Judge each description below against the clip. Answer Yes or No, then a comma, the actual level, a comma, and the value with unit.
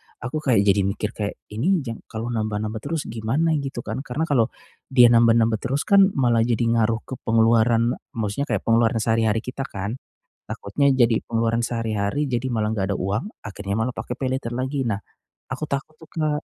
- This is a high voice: No, low, 115 Hz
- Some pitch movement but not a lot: Yes, average, 3.2 semitones